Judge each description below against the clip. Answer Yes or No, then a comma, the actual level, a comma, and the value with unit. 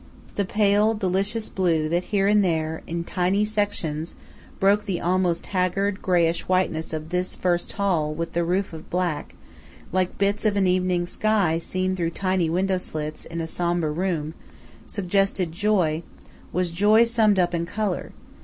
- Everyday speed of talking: Yes, average, 160 wpm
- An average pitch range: Yes, average, 3.0 semitones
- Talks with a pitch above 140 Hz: Yes, medium, 185 Hz